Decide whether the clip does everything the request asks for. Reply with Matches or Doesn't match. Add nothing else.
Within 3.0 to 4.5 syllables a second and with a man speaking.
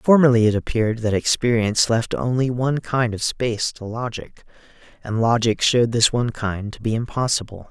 Doesn't match